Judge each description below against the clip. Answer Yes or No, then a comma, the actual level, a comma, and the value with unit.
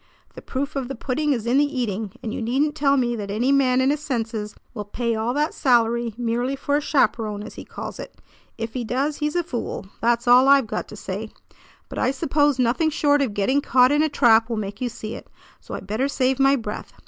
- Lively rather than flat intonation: No, average, 3.6 semitones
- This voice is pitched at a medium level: No, very high, 250 Hz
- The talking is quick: Yes, fast, 235 wpm